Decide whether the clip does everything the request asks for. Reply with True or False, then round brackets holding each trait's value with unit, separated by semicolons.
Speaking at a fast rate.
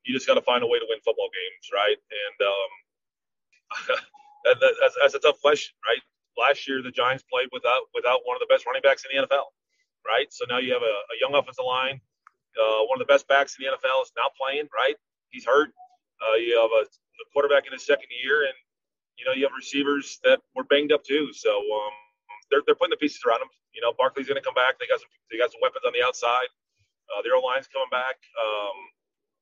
True (235 wpm)